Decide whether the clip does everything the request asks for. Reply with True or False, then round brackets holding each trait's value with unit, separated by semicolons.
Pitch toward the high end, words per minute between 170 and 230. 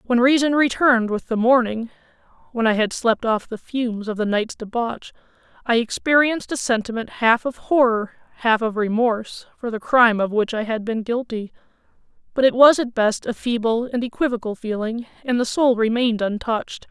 True (235 Hz; 175 wpm)